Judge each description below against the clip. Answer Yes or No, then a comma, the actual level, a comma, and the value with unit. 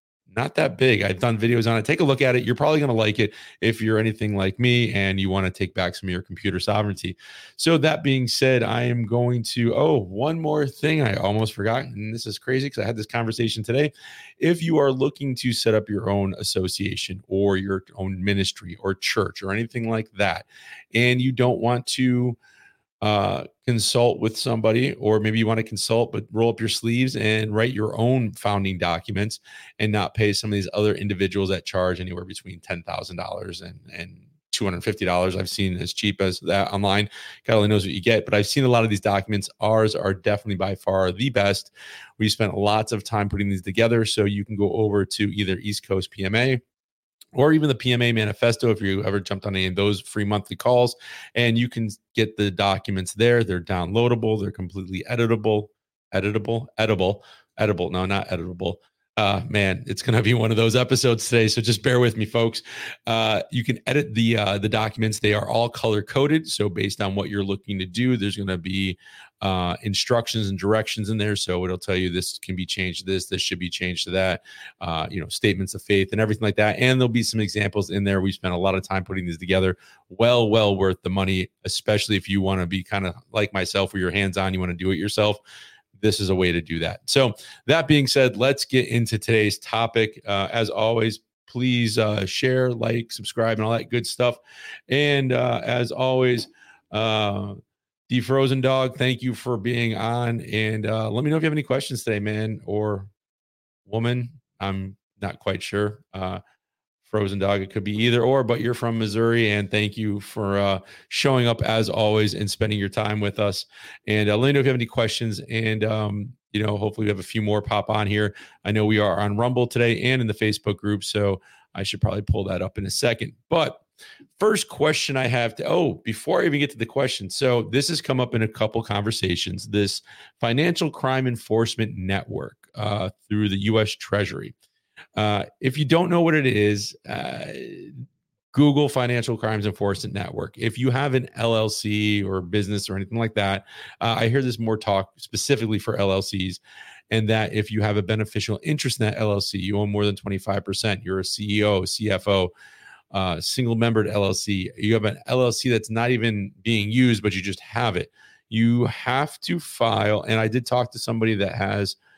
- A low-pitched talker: Yes, low, 110 Hz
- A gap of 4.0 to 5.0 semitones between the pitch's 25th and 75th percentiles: No, average, 3.1 semitones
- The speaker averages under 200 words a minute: No, fast, 205 wpm